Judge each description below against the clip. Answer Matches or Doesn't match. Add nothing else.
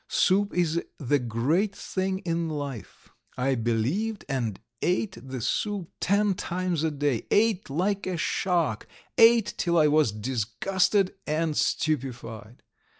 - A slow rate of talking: Matches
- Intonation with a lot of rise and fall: Matches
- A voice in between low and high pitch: Matches